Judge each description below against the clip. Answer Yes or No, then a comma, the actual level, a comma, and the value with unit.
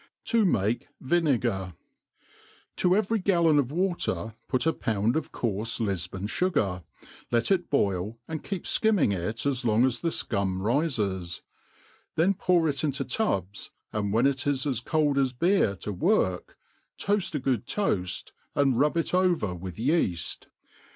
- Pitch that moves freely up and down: Yes, wide, 8.7 semitones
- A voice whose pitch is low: Yes, low, 130 Hz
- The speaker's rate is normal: Yes, average, 155 wpm